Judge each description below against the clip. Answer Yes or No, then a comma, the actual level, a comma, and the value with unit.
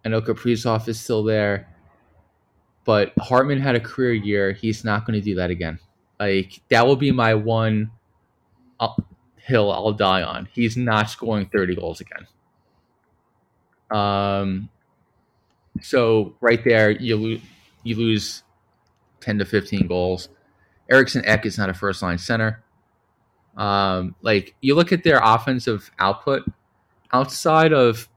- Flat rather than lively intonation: No, average, 3.0 semitones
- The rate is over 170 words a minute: No, average, 140 wpm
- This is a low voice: Yes, low, 110 Hz